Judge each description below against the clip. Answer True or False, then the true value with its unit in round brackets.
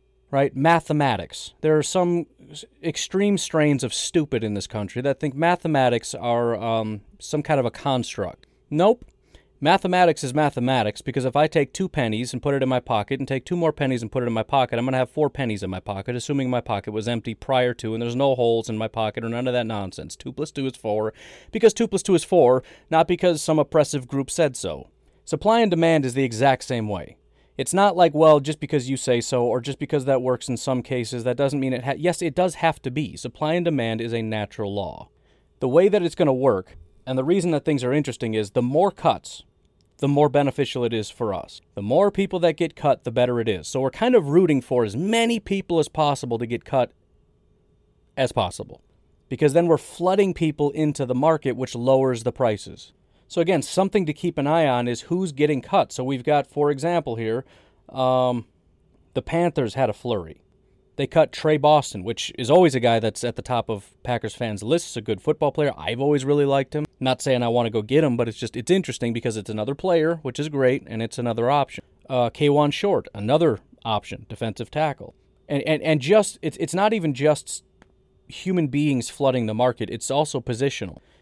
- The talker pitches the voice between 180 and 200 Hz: False (135 Hz)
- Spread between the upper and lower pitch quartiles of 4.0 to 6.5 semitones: True (4.7 semitones)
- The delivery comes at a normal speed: False (220 wpm)